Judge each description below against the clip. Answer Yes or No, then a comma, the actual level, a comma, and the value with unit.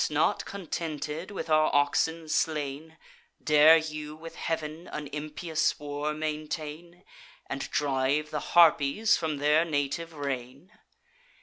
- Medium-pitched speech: Yes, medium, 155 Hz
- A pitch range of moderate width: No, narrow, 1.7 semitones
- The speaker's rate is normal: No, slow, 115 wpm